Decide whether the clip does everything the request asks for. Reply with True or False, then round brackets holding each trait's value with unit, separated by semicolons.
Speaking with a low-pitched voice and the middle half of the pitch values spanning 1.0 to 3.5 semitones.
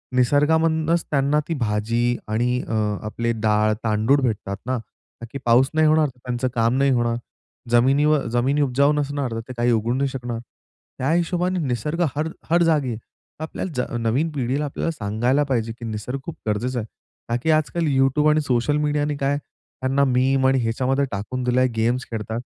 False (130 Hz; 3.9 semitones)